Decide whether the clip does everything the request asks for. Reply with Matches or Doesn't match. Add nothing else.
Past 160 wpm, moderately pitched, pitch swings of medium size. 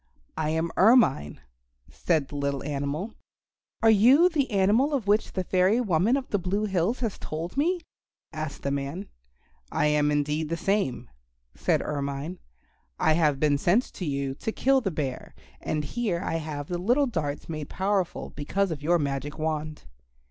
Doesn't match